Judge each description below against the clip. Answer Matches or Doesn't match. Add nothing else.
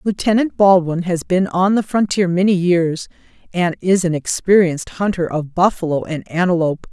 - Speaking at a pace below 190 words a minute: Matches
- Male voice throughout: Doesn't match